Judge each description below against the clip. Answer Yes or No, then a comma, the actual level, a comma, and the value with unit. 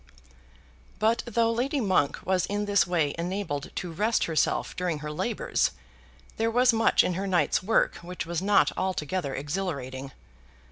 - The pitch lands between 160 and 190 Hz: Yes, medium, 185 Hz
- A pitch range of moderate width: Yes, average, 4.9 semitones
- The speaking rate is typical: Yes, average, 150 wpm